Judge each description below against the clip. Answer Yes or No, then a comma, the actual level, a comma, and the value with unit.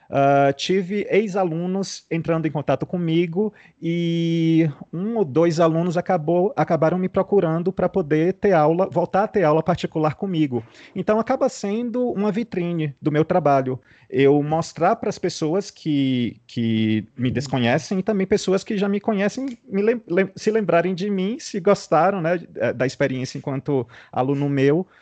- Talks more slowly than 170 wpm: Yes, average, 155 wpm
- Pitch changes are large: No, average, 4.6 semitones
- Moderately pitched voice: Yes, medium, 170 Hz